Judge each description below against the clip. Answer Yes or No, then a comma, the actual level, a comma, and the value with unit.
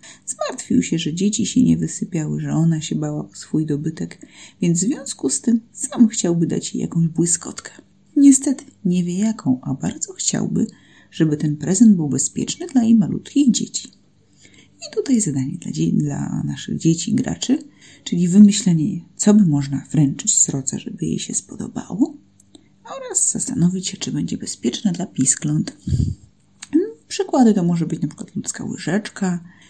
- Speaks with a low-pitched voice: No, high, 195 Hz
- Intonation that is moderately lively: No, wide, 6.7 semitones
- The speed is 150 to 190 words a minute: Yes, fast, 160 wpm